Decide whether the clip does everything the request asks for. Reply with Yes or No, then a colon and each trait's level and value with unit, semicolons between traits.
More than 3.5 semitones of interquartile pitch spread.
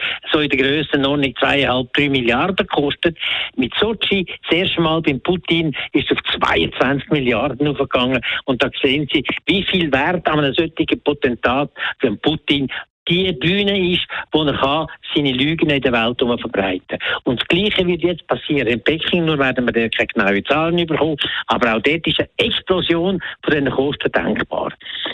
Yes: average, 4.0 semitones